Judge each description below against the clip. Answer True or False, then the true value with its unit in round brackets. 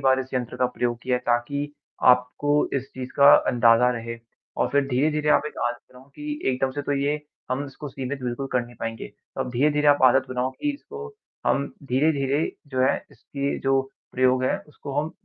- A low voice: True (130 Hz)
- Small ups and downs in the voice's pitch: True (2.3 semitones)